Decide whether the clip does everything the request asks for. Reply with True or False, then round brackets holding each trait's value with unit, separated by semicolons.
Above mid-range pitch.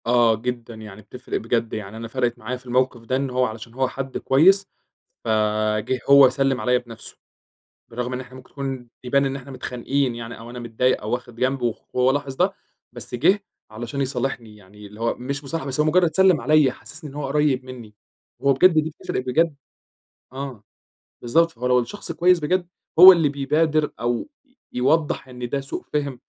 False (130 Hz)